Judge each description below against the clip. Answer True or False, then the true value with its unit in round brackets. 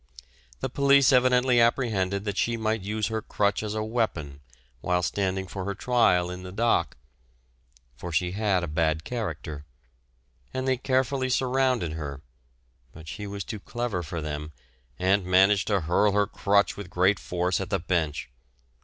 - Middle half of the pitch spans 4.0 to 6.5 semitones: True (4.7 semitones)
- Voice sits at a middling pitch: False (100 Hz)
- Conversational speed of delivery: True (160 wpm)